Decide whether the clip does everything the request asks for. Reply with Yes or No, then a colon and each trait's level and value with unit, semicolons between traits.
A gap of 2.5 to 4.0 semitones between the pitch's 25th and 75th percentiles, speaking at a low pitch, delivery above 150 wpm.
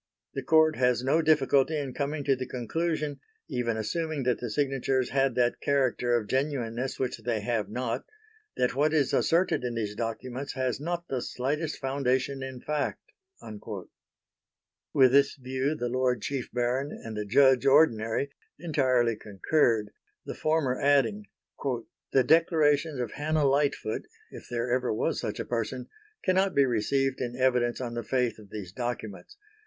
Yes: average, 3.0 semitones; low, 130 Hz; average, 160 wpm